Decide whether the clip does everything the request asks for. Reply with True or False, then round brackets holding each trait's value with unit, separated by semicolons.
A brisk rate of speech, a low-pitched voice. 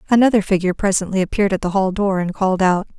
False (220 wpm; 195 Hz)